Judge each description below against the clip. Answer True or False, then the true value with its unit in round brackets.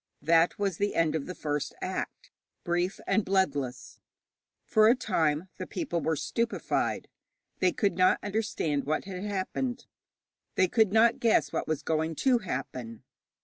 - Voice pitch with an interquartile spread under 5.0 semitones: False (5.3 semitones)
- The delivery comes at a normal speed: True (150 wpm)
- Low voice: False (185 Hz)